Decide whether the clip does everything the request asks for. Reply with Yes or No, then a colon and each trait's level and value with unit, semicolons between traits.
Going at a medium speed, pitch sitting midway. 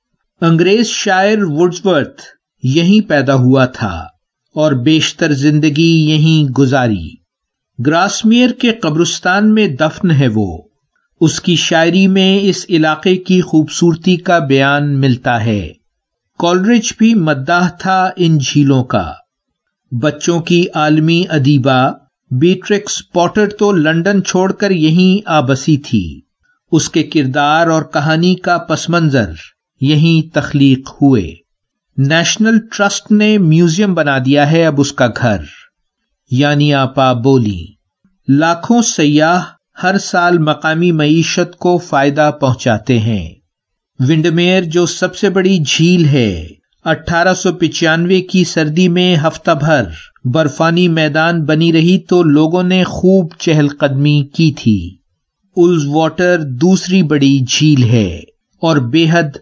No: slow, 120 wpm; medium, 160 Hz